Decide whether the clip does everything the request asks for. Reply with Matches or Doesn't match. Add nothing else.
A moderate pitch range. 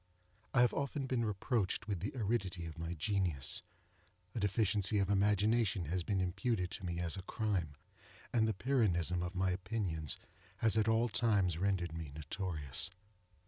Matches